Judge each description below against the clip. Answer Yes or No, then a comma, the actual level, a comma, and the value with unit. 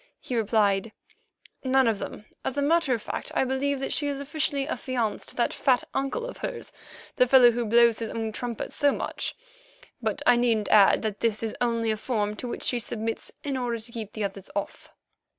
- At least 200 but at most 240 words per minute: Yes, fast, 205 wpm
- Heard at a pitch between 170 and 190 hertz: No, high, 235 Hz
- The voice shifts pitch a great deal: No, average, 3.4 semitones